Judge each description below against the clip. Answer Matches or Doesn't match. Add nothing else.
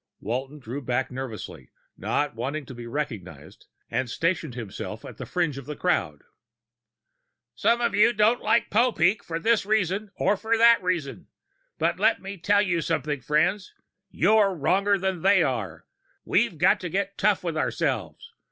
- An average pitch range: Doesn't match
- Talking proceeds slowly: Doesn't match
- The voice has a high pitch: Doesn't match